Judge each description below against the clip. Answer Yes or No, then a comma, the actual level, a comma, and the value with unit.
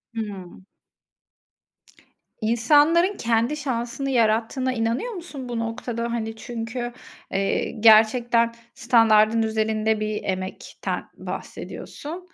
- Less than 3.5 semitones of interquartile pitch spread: Yes, narrow, 2.6 semitones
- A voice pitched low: No, high, 230 Hz